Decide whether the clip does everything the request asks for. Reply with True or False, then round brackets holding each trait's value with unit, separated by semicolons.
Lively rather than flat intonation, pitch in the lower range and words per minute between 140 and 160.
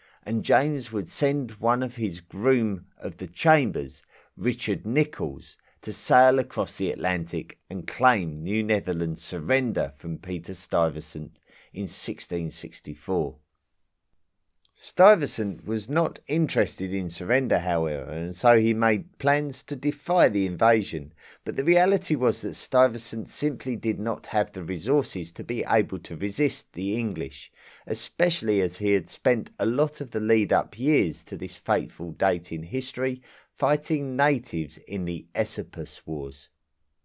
True (7.2 semitones; 105 Hz; 145 wpm)